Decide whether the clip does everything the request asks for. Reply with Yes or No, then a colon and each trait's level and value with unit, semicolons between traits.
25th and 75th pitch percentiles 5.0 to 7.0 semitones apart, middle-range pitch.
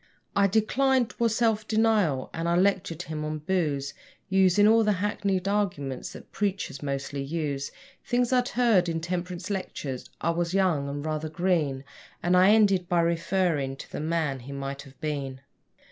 Yes: wide, 5.6 semitones; medium, 175 Hz